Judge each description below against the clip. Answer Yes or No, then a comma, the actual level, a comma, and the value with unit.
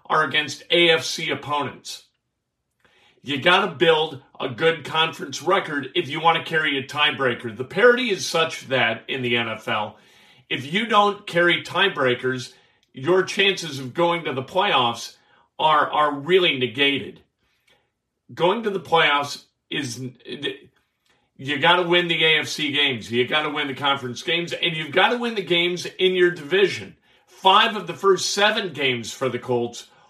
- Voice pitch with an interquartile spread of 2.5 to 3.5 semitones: No, average, 5.0 semitones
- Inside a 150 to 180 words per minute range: Yes, average, 160 wpm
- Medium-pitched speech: Yes, medium, 155 Hz